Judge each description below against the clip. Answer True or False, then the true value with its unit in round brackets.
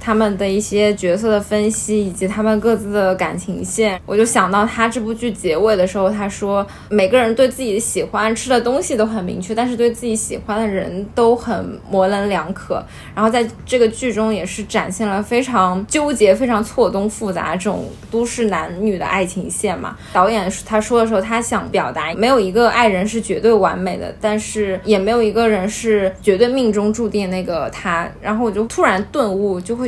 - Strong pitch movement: False (2.7 semitones)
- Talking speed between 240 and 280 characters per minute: False (305 characters per minute)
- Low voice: False (215 Hz)